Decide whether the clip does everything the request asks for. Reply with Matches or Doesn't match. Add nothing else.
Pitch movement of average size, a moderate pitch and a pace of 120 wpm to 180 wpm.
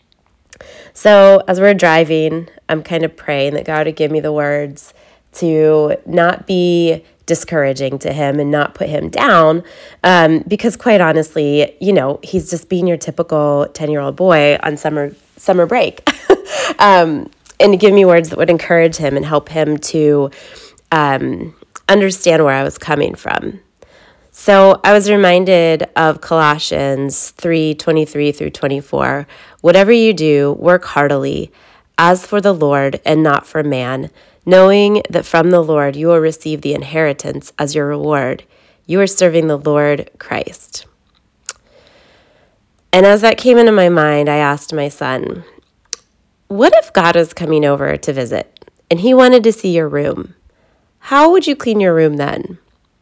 Matches